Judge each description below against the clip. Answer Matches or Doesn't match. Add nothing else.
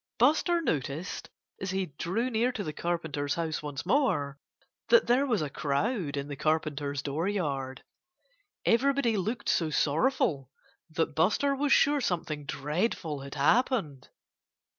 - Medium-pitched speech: Matches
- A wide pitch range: Matches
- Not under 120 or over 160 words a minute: Matches